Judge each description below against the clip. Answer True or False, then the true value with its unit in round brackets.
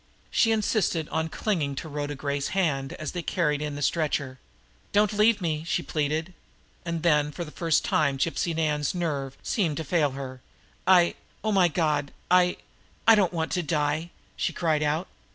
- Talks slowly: False (175 wpm)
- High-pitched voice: False (160 Hz)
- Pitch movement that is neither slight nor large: True (3.3 semitones)